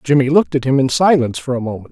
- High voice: No, low, 135 Hz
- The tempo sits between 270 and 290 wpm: Yes, fast, 280 wpm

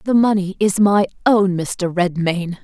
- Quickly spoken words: No, average, 160 wpm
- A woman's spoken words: Yes, female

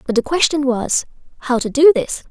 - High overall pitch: Yes, very high, 275 Hz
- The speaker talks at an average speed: No, fast, 210 wpm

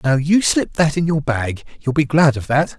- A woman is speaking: No, male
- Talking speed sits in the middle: No, fast, 260 wpm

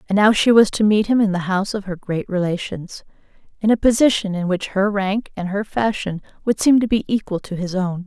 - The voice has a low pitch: No, high, 200 Hz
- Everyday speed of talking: No, fast, 230 wpm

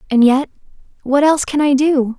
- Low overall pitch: No, very high, 275 Hz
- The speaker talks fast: No, average, 190 wpm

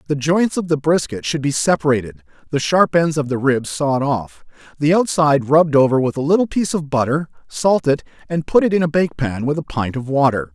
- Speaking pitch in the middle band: Yes, medium, 145 Hz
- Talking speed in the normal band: No, fast, 220 wpm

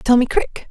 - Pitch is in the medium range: No, high, 245 Hz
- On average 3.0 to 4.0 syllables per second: No, 4.5 syllables/s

